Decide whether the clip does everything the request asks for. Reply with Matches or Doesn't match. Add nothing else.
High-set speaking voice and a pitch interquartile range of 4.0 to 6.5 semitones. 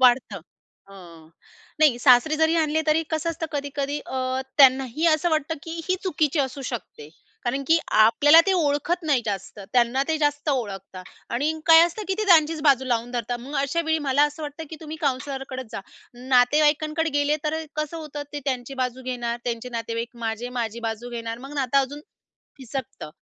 Matches